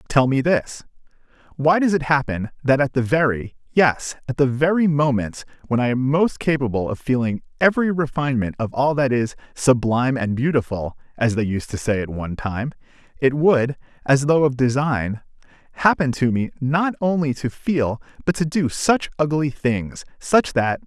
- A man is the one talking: Yes, male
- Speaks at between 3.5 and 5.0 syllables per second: Yes, 4.8 syllables/s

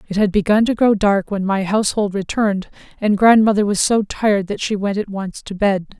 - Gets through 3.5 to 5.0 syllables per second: No, 5.5 syllables/s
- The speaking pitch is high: Yes, high, 205 Hz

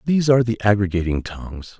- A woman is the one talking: No, male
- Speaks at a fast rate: No, average, 165 wpm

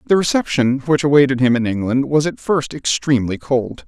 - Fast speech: No, average, 185 wpm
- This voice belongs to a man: Yes, male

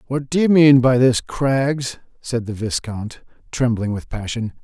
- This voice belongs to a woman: No, male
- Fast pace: No, average, 170 wpm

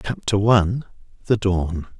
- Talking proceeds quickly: No, slow, 90 wpm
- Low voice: Yes, low, 100 Hz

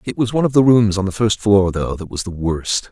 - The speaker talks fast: Yes, fast, 310 wpm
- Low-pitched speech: Yes, low, 100 Hz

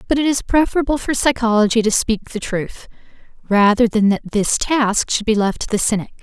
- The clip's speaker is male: No, female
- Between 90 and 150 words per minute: No, average, 200 wpm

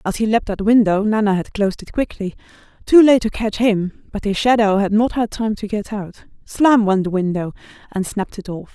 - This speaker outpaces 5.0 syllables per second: Yes, 5.4 syllables/s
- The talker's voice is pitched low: No, high, 210 Hz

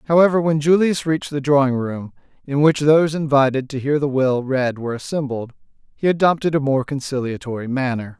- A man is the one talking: Yes, male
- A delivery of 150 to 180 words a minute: Yes, average, 175 wpm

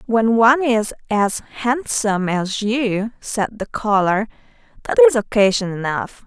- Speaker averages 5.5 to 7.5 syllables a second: No, 4.0 syllables/s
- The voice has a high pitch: Yes, high, 220 Hz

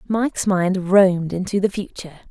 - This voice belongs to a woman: Yes, female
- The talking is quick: No, average, 155 wpm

